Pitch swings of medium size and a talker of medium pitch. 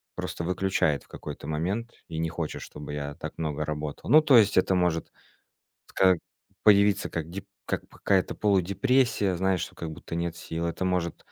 No: average, 3.5 semitones; very low, 90 Hz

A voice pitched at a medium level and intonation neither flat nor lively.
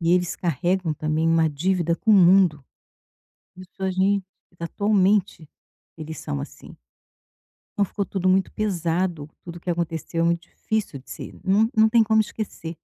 Yes: medium, 180 Hz; average, 3.1 semitones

